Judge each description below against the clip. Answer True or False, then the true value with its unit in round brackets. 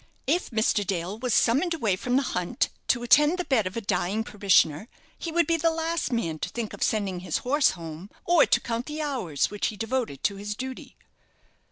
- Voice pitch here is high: True (230 Hz)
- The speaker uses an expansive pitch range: True (6.7 semitones)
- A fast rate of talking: True (210 wpm)